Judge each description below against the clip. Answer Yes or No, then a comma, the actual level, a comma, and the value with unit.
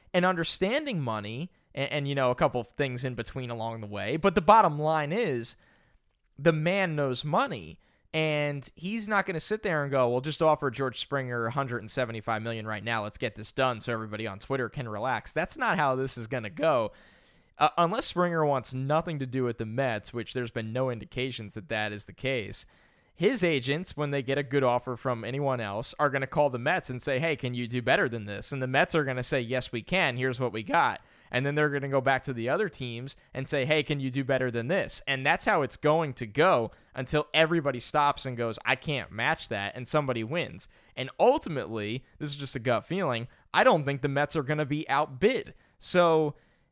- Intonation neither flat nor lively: Yes, average, 4.0 semitones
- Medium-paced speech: No, fast, 230 wpm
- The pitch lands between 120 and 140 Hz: Yes, low, 135 Hz